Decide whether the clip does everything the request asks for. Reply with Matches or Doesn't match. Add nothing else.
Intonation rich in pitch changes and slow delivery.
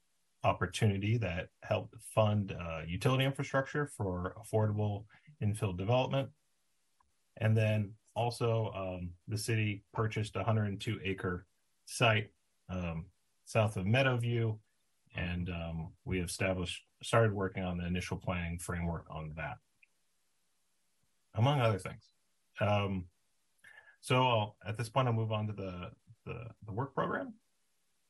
Doesn't match